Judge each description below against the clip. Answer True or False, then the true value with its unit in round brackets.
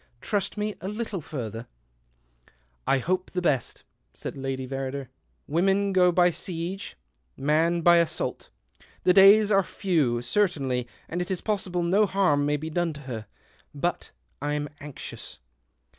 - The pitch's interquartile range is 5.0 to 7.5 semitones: True (5.5 semitones)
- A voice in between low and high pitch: True (170 Hz)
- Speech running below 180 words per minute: True (150 wpm)